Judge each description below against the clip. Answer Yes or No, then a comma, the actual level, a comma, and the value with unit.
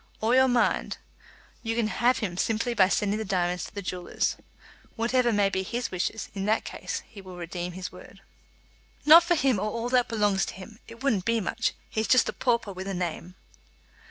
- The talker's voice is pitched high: Yes, high, 215 Hz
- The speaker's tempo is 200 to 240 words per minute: Yes, fast, 205 wpm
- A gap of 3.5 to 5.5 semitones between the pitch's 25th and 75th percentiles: Yes, average, 3.9 semitones